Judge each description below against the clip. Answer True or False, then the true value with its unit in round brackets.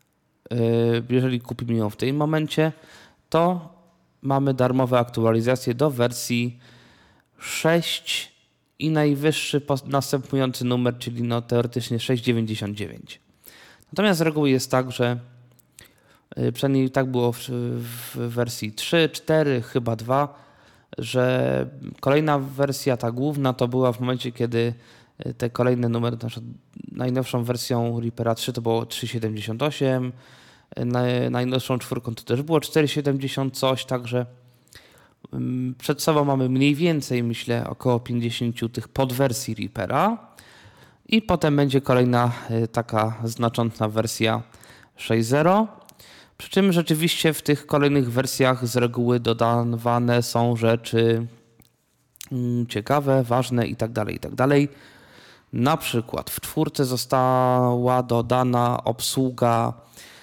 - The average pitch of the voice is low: True (125 Hz)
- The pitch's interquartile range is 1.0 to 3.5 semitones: True (2.6 semitones)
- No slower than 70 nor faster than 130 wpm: True (110 wpm)